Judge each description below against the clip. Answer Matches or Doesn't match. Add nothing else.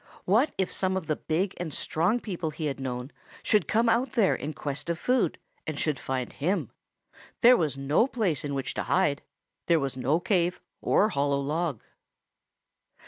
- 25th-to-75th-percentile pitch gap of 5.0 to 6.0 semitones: Matches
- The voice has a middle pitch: Matches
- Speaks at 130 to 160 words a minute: Doesn't match